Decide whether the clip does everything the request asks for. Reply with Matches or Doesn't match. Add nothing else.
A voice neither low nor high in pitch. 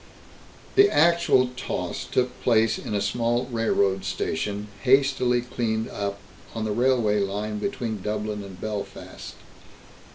Doesn't match